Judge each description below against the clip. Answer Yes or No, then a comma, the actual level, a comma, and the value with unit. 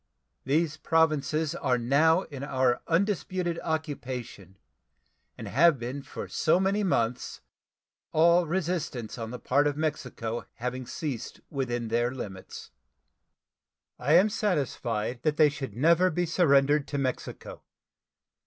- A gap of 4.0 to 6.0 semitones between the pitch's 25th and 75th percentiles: Yes, average, 4.7 semitones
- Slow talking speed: Yes, slow, 125 wpm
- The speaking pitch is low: No, medium, 145 Hz